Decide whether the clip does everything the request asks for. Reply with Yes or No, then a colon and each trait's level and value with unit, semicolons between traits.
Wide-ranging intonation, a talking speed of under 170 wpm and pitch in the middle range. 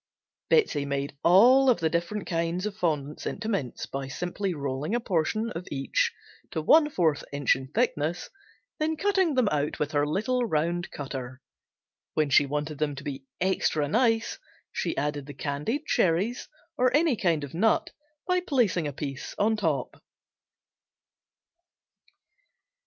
Yes: wide, 7.7 semitones; average, 150 wpm; medium, 170 Hz